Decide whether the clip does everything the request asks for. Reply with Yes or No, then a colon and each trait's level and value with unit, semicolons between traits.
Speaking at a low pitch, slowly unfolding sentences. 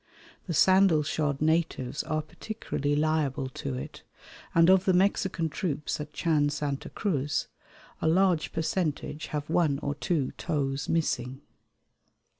No: medium, 155 Hz; slow, 130 wpm